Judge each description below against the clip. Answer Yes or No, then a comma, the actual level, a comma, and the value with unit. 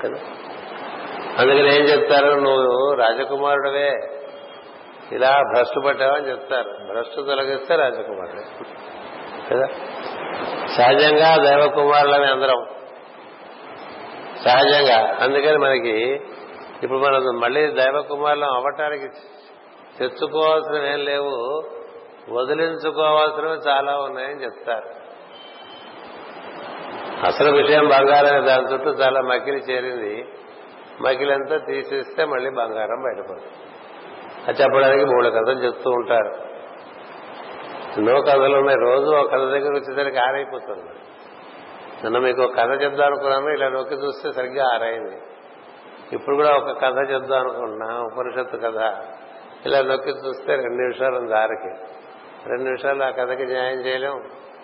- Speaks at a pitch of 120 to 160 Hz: Yes, medium, 140 Hz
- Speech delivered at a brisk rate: No, average, 100 wpm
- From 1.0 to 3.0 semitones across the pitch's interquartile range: Yes, narrow, 2.6 semitones